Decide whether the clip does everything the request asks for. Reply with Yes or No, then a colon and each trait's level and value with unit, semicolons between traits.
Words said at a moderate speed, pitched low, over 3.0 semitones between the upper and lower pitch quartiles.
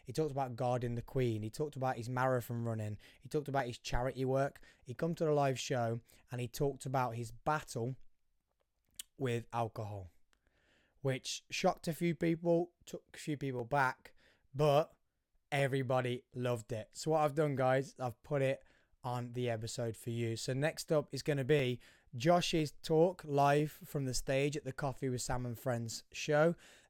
Yes: average, 180 wpm; low, 130 Hz; average, 3.7 semitones